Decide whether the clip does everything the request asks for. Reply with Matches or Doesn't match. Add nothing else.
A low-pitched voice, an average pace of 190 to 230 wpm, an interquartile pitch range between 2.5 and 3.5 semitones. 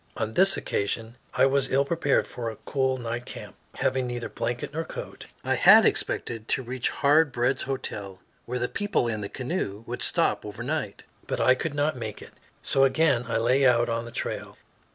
Matches